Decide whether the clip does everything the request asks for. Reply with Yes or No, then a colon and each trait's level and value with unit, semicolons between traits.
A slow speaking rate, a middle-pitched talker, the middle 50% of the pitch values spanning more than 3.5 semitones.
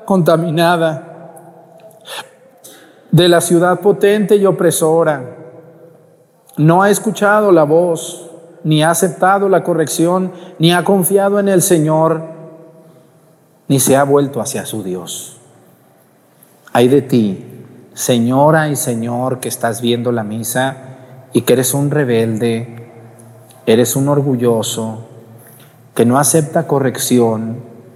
Yes: slow, 115 wpm; medium, 155 Hz; wide, 5.5 semitones